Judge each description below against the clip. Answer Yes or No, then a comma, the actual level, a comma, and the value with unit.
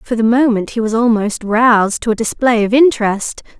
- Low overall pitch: No, high, 230 Hz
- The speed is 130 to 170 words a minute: No, average, 200 wpm